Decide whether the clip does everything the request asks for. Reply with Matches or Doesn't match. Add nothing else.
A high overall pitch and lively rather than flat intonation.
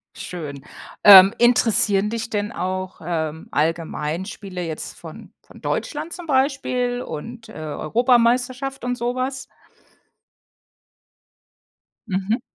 Matches